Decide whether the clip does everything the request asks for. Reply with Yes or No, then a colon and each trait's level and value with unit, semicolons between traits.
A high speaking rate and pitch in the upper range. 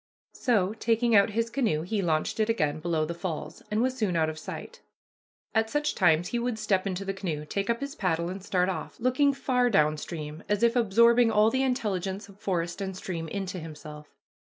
Yes: fast, 210 wpm; high, 195 Hz